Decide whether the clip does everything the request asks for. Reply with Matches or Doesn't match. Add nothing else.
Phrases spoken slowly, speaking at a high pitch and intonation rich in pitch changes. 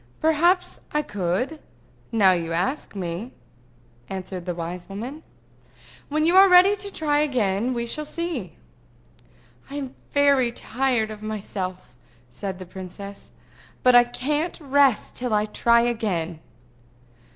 Matches